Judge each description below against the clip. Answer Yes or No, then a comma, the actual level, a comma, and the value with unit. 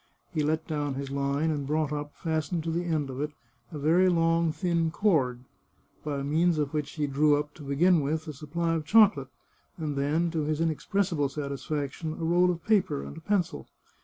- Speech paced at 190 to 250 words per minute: Yes, average, 200 wpm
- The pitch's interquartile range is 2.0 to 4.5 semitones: Yes, narrow, 2.6 semitones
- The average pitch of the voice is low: No, medium, 155 Hz